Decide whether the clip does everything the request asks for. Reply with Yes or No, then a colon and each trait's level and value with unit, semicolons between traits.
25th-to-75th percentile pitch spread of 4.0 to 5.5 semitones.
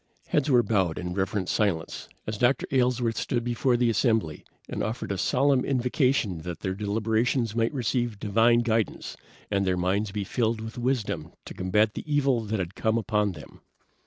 No: average, 3.5 semitones